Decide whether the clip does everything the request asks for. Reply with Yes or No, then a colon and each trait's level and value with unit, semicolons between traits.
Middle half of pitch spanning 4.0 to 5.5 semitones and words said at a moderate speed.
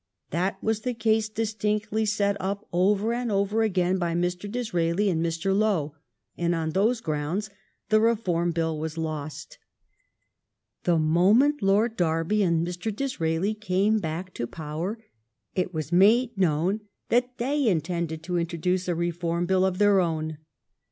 Yes: average, 4.3 semitones; average, 150 wpm